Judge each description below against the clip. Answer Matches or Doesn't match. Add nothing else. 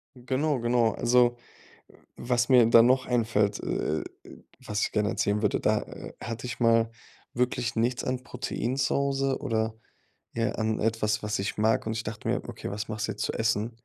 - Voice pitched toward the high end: Doesn't match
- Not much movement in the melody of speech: Matches